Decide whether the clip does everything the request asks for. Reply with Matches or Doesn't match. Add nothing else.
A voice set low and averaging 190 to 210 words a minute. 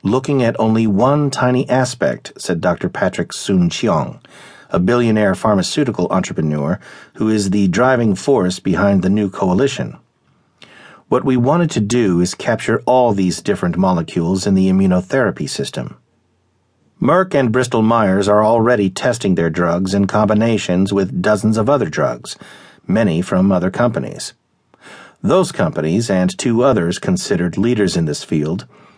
Doesn't match